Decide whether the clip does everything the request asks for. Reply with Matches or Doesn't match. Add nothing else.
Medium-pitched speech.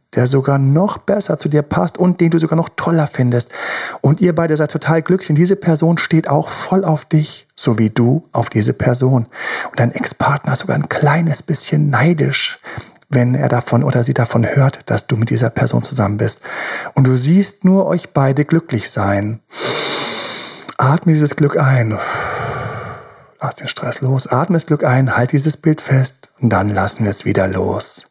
Matches